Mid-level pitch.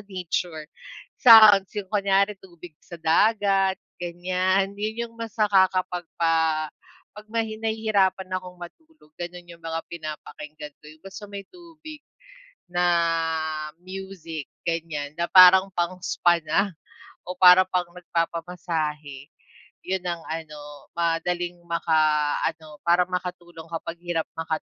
Yes: medium, 175 Hz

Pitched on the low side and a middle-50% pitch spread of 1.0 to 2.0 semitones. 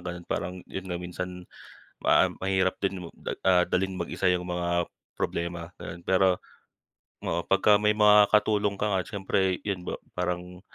Yes: very low, 90 Hz; narrow, 1.7 semitones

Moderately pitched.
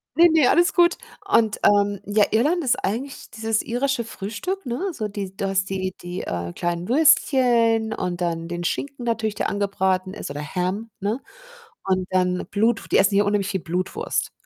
No: high, 205 Hz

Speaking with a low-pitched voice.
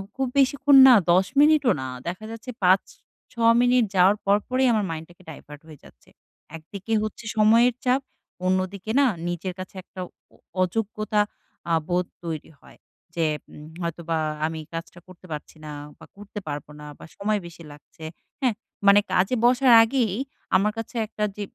No: high, 200 Hz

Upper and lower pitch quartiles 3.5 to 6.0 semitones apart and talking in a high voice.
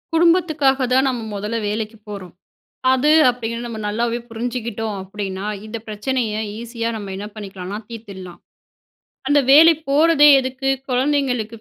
Yes: average, 4.2 semitones; high, 235 Hz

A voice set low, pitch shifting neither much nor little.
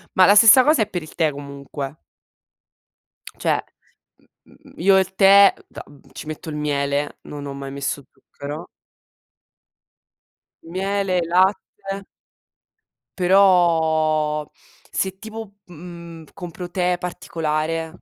No: medium, 170 Hz; average, 4.0 semitones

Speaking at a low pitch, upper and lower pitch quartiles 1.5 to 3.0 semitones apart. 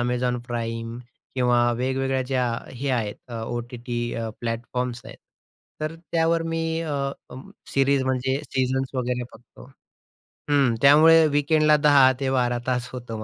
Yes: low, 130 Hz; narrow, 2.5 semitones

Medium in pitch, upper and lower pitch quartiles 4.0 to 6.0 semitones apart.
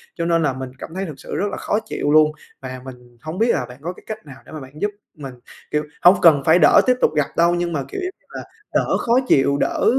Yes: medium, 155 Hz; average, 4.4 semitones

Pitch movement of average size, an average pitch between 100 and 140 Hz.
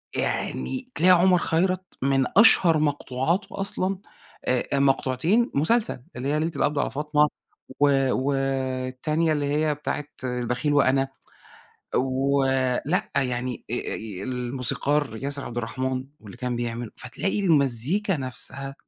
Yes: average, 3.4 semitones; low, 135 Hz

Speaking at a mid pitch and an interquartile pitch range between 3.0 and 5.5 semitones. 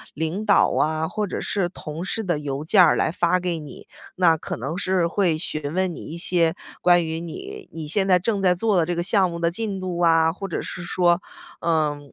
No: medium, 175 Hz; narrow, 2.6 semitones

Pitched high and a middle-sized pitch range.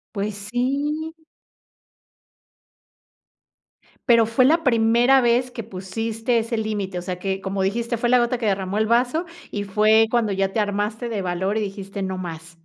Yes: high, 220 Hz; average, 3.5 semitones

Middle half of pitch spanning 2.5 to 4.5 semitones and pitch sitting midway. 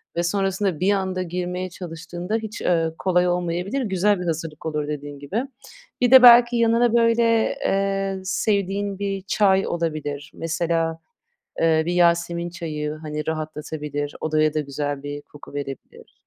Yes: average, 4.1 semitones; medium, 175 Hz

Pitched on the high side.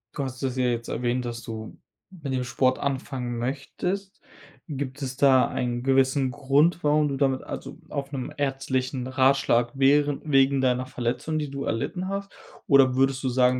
No: low, 135 Hz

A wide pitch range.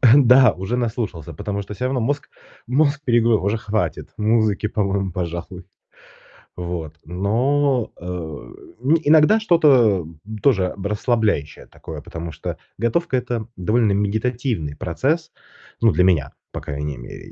Yes: wide, 5.7 semitones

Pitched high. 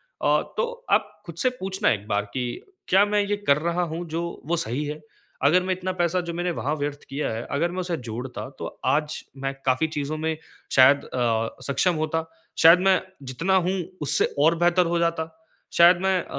No: medium, 165 Hz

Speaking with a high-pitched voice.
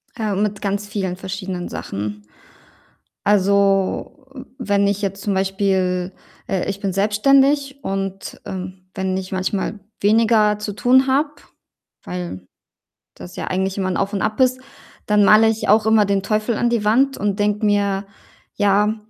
Yes: high, 200 Hz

